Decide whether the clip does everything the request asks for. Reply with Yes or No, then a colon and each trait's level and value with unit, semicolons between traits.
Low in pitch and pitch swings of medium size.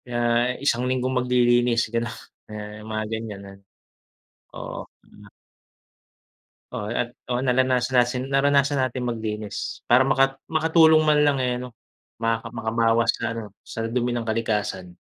No: low, 120 Hz; narrow, 2.3 semitones